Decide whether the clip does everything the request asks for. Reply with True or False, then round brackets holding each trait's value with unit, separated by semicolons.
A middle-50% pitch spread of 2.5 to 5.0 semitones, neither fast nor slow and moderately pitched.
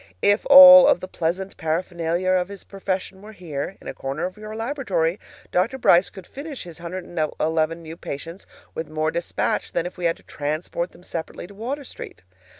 True (3.6 semitones; 190 wpm; 180 Hz)